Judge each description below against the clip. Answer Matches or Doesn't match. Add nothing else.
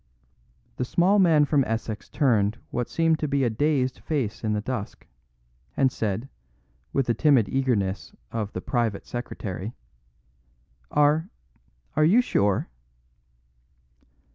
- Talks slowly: Matches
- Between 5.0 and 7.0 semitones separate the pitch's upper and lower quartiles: Matches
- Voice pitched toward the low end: Matches